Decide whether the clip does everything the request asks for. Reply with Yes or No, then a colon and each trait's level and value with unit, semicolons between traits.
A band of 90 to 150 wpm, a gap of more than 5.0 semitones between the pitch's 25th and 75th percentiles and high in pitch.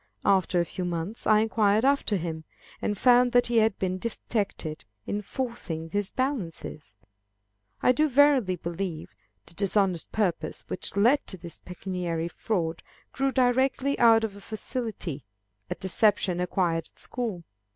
Yes: average, 145 wpm; wide, 5.4 semitones; high, 200 Hz